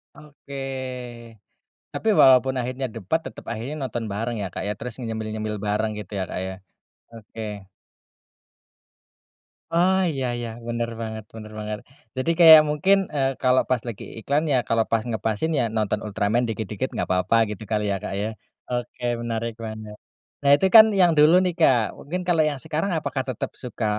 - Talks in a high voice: No, low, 115 Hz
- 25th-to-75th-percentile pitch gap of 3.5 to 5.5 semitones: Yes, average, 4.6 semitones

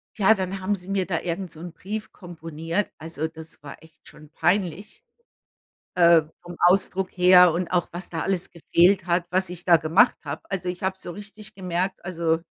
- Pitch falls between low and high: Yes, medium, 180 Hz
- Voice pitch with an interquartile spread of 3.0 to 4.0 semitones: No, narrow, 2.4 semitones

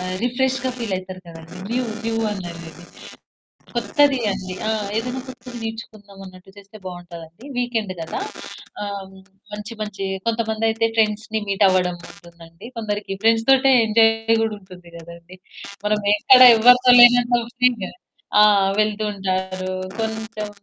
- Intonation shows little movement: No, average, 3.6 semitones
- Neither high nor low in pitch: No, high, 215 Hz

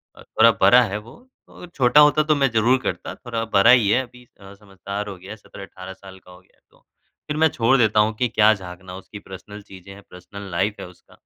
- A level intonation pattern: No, average, 4.1 semitones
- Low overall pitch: Yes, low, 105 Hz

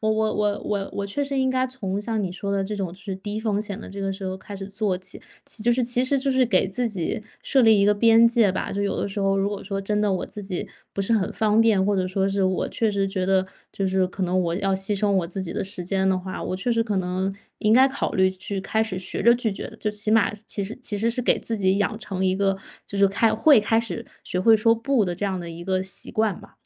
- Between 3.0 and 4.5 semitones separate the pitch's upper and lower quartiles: No, narrow, 2.6 semitones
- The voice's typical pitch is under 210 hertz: Yes, high, 200 Hz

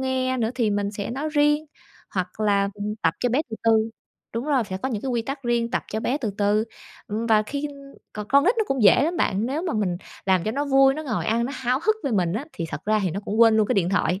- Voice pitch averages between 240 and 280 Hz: No, high, 230 Hz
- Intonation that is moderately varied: Yes, average, 4.6 semitones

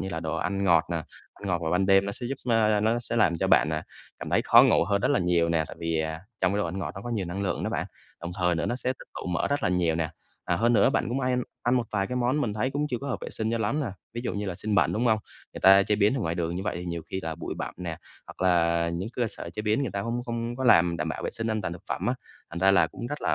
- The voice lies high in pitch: No, low, 100 Hz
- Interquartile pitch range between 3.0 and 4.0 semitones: No, average, 5.3 semitones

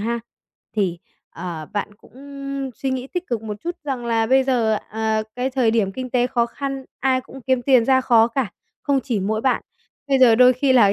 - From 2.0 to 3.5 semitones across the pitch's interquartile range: Yes, average, 3.0 semitones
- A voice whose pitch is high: Yes, high, 245 Hz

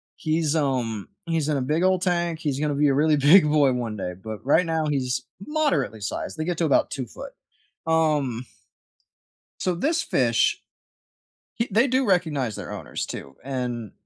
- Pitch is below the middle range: No, medium, 150 Hz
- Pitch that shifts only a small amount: No, average, 4.8 semitones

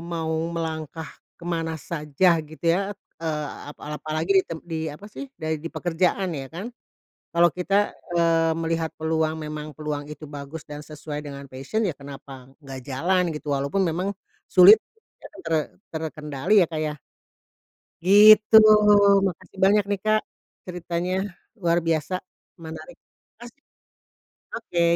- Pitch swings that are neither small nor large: Yes, average, 3.2 semitones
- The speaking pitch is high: No, medium, 165 Hz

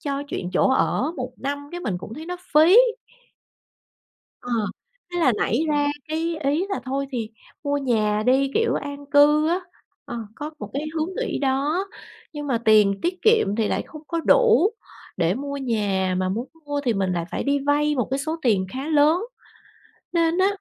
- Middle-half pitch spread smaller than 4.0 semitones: No, average, 5.1 semitones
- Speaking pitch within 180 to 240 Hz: No, very high, 285 Hz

